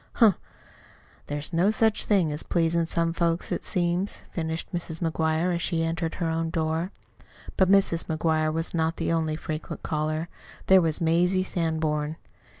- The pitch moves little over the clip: Yes, narrow, 1.6 semitones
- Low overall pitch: No, medium, 165 Hz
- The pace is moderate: Yes, average, 155 wpm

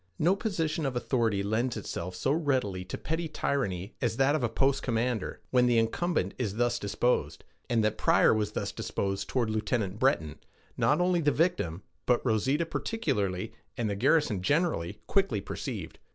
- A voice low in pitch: Yes, low, 120 Hz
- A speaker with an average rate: Yes, average, 165 wpm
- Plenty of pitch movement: Yes, wide, 6.2 semitones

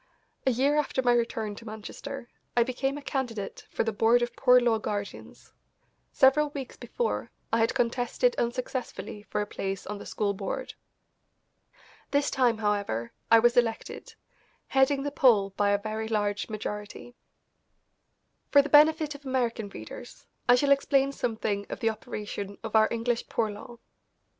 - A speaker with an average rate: Yes, average, 155 wpm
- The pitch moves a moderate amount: Yes, average, 4.1 semitones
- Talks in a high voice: Yes, high, 235 Hz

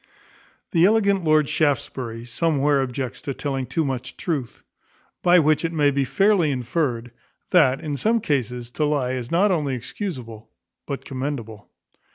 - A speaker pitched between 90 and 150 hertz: Yes, medium, 140 Hz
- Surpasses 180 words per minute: No, average, 150 wpm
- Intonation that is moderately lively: Yes, average, 4.5 semitones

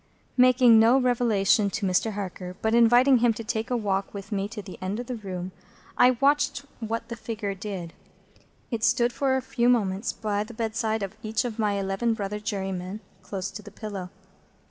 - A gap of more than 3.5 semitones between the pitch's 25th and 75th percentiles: No, average, 3.2 semitones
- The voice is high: Yes, high, 220 Hz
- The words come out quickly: No, average, 190 wpm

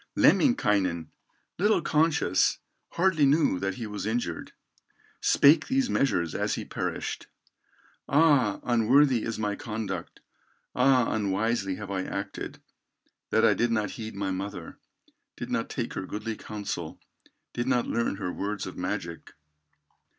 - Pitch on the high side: No, low, 110 Hz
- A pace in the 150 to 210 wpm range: No, slow, 135 wpm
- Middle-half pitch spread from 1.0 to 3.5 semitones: No, average, 5.2 semitones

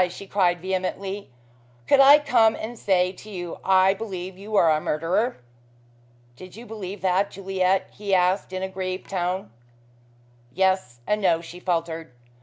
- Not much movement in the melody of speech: Yes, narrow, 1.9 semitones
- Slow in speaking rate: No, average, 155 wpm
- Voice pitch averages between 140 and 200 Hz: Yes, high, 190 Hz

